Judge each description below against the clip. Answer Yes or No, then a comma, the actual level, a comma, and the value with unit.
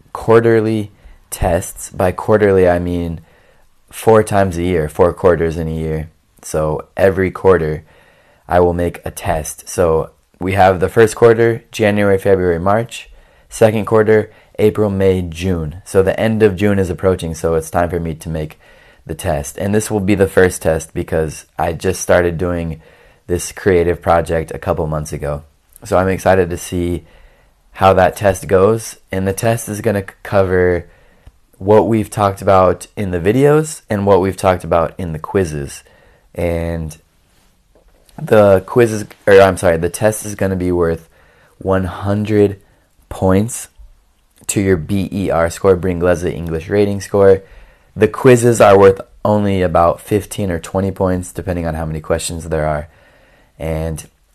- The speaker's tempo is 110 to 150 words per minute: No, average, 160 wpm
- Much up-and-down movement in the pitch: No, average, 3.4 semitones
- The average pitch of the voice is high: No, very low, 95 Hz